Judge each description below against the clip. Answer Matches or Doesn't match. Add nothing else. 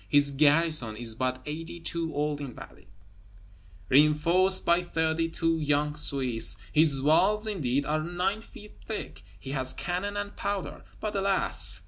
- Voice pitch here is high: Doesn't match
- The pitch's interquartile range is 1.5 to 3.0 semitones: Doesn't match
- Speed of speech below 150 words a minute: Matches